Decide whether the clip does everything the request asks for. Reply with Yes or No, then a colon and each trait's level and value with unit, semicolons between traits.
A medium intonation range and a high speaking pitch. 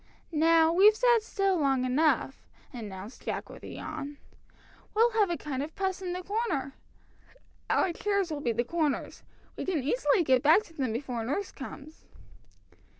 No: wide, 6.3 semitones; very high, 320 Hz